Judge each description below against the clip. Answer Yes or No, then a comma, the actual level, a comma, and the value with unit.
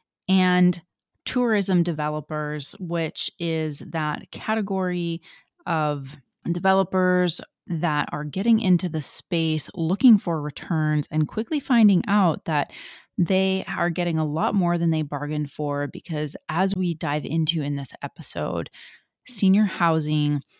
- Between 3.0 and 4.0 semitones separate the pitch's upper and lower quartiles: Yes, average, 3.7 semitones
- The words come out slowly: Yes, slow, 125 wpm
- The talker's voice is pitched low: No, medium, 170 Hz